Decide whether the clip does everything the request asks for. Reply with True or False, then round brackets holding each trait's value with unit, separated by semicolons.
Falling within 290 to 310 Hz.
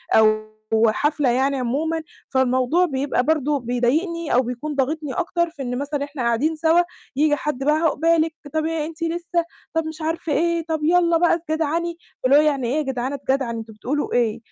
True (300 Hz)